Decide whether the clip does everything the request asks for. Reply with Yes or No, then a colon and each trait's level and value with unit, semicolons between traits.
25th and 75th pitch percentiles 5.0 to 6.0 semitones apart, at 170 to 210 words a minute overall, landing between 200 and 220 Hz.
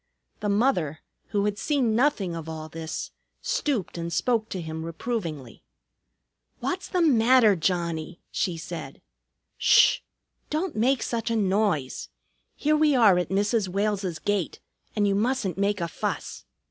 No: wide, 5.6 semitones; average, 145 wpm; high, 205 Hz